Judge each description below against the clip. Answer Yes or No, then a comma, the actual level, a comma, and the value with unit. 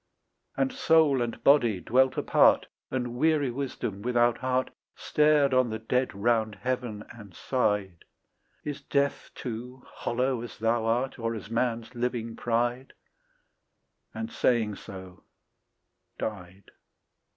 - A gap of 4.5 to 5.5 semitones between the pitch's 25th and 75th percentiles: No, average, 2.8 semitones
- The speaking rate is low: Yes, slow, 120 wpm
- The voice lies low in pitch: Yes, low, 120 Hz